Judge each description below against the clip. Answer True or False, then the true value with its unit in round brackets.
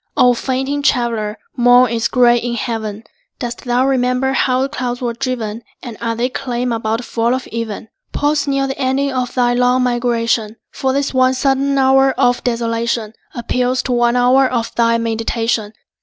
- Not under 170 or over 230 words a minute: True (175 wpm)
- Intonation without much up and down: True (2.0 semitones)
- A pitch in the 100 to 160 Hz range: False (245 Hz)